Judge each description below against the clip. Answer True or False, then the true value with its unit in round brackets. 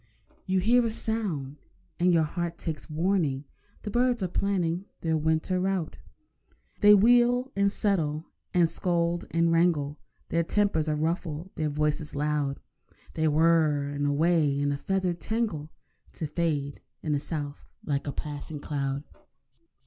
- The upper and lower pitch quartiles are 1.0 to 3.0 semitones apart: False (4.0 semitones)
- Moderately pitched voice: True (165 Hz)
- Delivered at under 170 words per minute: True (140 wpm)